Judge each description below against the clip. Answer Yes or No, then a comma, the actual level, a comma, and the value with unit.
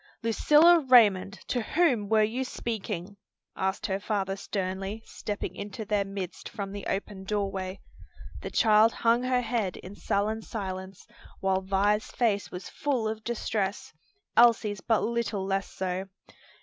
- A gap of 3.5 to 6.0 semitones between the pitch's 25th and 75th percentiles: No, average, 2.9 semitones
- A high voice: Yes, high, 205 Hz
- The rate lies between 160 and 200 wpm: No, average, 145 wpm